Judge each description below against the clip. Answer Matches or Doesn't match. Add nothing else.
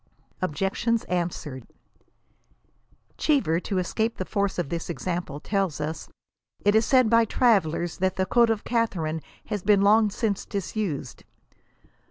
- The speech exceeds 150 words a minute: Doesn't match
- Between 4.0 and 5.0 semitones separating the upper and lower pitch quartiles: Matches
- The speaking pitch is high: Matches